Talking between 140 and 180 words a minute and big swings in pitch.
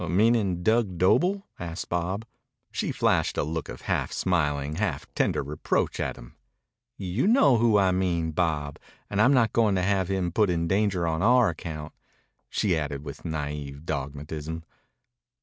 No: average, 160 wpm; average, 5.0 semitones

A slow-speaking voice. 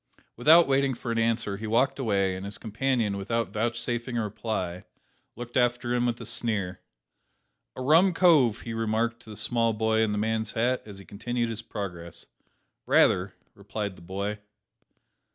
No: average, 170 wpm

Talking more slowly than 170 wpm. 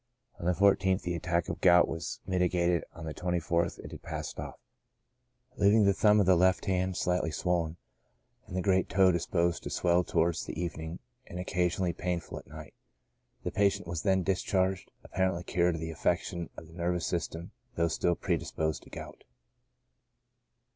No: average, 175 wpm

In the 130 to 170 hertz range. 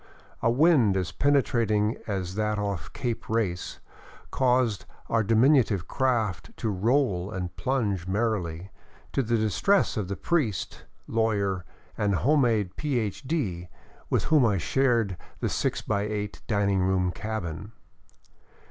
No: low, 105 Hz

